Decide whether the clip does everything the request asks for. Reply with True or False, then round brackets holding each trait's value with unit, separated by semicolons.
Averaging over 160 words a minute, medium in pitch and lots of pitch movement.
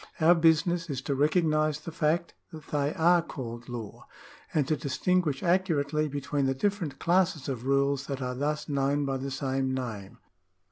False (170 wpm; 145 Hz; 3.2 semitones)